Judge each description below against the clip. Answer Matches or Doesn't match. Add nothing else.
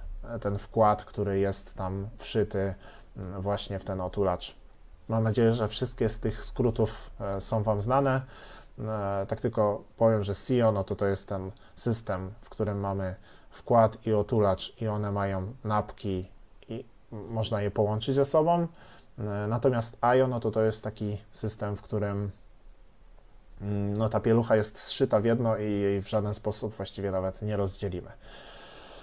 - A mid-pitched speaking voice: Doesn't match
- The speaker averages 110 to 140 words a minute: Doesn't match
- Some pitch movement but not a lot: Doesn't match